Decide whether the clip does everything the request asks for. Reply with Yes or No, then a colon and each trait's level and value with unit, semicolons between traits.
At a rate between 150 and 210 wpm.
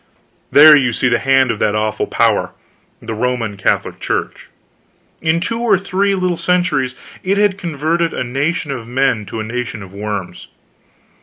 Yes: average, 165 wpm